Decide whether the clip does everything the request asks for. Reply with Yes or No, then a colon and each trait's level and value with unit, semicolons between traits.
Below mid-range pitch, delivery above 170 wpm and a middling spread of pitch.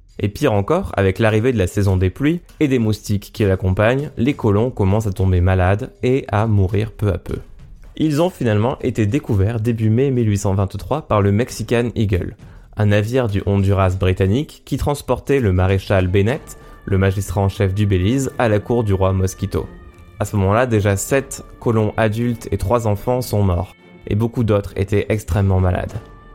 Yes: low, 105 Hz; average, 180 wpm; average, 3.6 semitones